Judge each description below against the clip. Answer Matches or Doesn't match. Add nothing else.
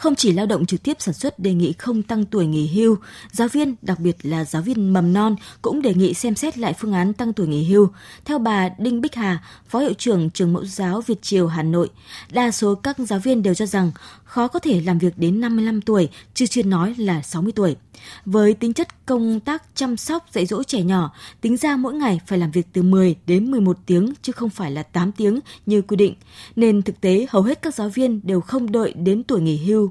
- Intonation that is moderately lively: Matches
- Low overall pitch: Doesn't match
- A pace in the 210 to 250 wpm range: Matches